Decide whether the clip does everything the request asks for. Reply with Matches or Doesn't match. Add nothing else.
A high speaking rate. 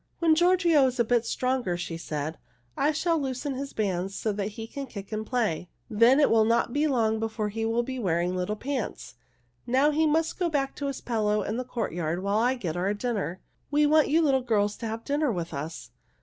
Matches